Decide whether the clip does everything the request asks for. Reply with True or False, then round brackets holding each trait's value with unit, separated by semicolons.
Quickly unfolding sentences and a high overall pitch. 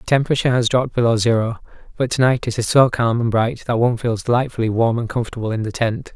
False (245 wpm; 120 Hz)